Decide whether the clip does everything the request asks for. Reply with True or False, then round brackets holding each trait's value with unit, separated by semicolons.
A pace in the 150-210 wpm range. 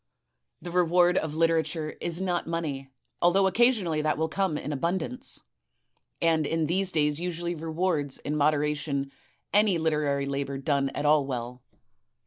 False (140 wpm)